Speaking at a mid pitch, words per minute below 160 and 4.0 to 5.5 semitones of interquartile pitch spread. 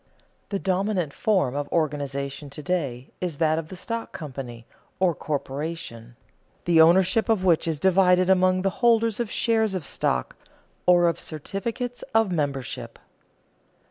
Yes: medium, 175 Hz; average, 140 wpm; average, 5.0 semitones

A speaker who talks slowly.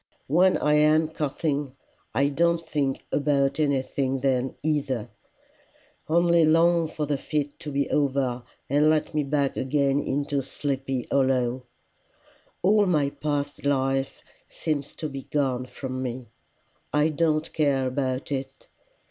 Yes: slow, 130 wpm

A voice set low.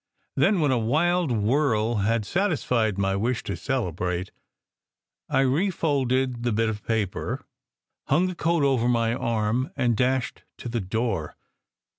Yes: low, 120 Hz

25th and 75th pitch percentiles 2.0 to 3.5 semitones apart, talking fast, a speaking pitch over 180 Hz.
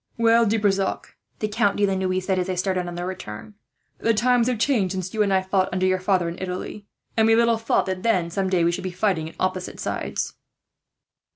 Yes: average, 2.8 semitones; fast, 230 wpm; high, 190 Hz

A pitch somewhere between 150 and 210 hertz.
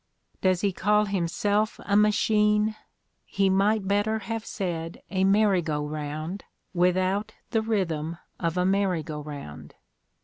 Yes: high, 190 Hz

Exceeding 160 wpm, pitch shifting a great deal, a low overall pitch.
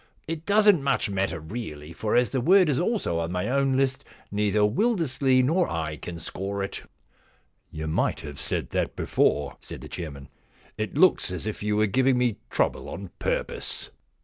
Yes: average, 190 wpm; wide, 7.9 semitones; low, 110 Hz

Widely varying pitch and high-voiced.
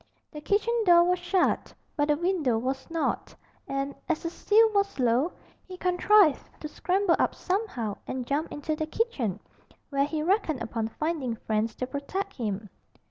Yes: wide, 6.1 semitones; very high, 310 Hz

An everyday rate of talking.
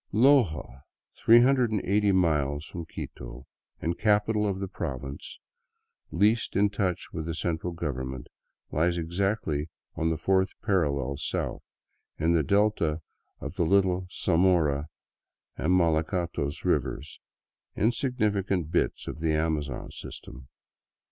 No: slow, 115 wpm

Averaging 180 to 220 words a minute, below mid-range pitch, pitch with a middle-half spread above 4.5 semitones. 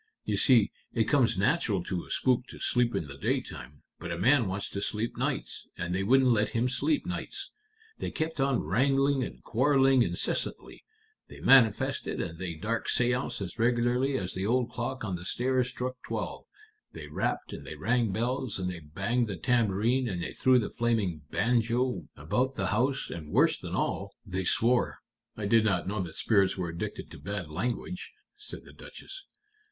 Yes: average, 185 wpm; low, 115 Hz; average, 5.0 semitones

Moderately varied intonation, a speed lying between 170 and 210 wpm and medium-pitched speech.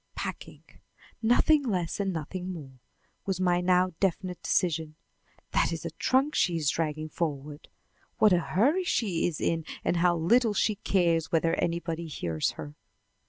No: average, 3.2 semitones; average, 155 wpm; medium, 175 Hz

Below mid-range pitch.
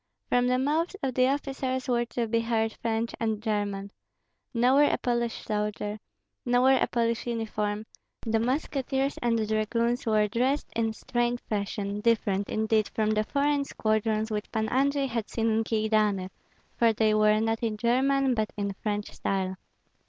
No: high, 225 Hz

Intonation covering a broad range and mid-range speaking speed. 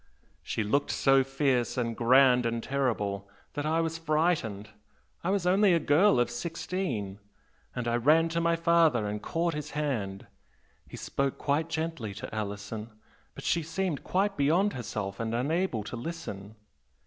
Yes: wide, 6.4 semitones; average, 160 wpm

